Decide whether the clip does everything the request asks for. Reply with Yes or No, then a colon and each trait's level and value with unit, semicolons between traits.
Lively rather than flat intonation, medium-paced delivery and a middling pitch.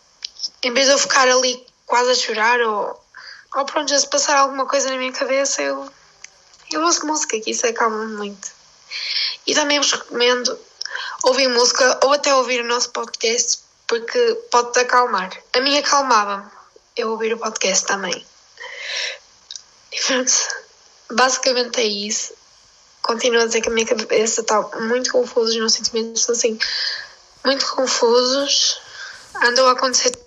No: wide, 8.2 semitones; average, 150 wpm; very high, 265 Hz